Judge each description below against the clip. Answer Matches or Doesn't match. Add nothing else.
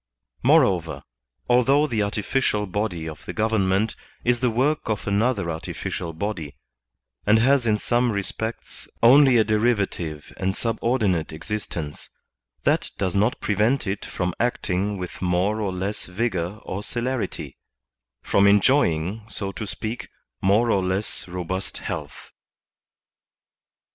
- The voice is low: Matches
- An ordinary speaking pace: Doesn't match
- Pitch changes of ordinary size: Matches